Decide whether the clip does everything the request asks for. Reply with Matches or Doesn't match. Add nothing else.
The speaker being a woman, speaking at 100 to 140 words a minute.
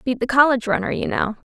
Doesn't match